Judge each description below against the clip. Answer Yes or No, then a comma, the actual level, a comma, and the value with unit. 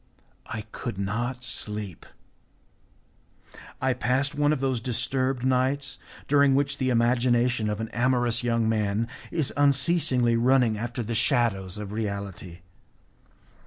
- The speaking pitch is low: Yes, low, 120 Hz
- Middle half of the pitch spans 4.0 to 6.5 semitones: No, average, 3.1 semitones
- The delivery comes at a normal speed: No, slow, 125 wpm